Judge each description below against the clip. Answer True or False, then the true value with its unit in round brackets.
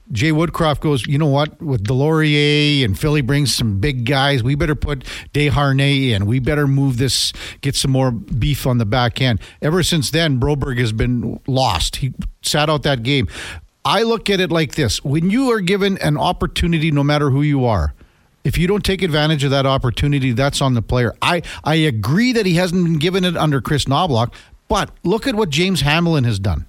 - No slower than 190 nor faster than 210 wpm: True (205 wpm)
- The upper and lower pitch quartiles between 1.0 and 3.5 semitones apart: False (4.2 semitones)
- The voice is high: False (140 Hz)